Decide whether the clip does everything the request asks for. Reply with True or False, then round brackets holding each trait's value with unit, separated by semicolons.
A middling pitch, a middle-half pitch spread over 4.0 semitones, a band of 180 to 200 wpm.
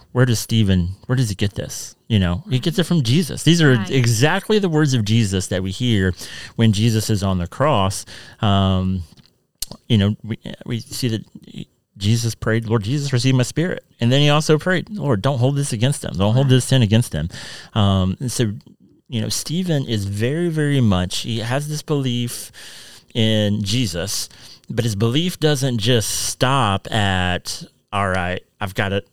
False (115 Hz; 4.9 semitones; 185 wpm)